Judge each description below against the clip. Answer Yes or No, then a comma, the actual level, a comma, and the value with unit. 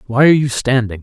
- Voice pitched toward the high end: No, low, 125 Hz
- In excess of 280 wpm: No, fast, 235 wpm